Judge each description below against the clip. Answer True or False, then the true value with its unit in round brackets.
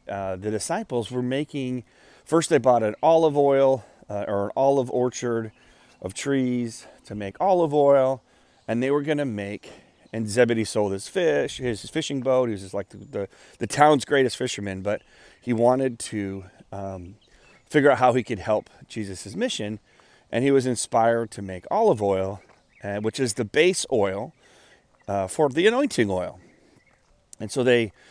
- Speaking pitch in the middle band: False (120 Hz)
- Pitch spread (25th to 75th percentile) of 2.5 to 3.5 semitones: False (4.7 semitones)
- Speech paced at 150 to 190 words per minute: True (175 wpm)